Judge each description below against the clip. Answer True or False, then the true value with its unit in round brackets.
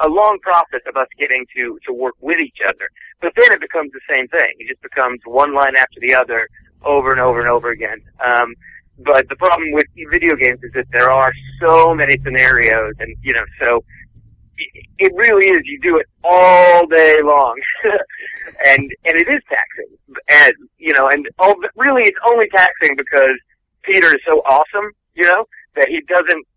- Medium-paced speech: True (195 wpm)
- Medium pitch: True (160 Hz)